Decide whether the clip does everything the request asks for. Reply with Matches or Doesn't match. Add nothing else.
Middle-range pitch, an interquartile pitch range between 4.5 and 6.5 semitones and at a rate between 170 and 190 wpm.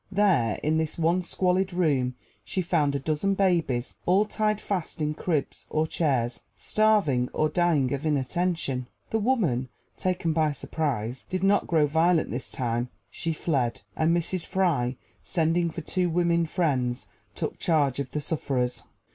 Doesn't match